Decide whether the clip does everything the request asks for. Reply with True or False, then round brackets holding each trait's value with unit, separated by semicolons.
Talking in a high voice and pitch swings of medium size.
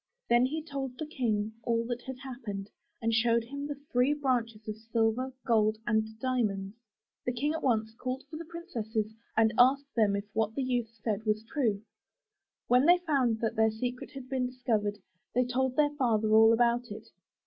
True (240 Hz; 3.1 semitones)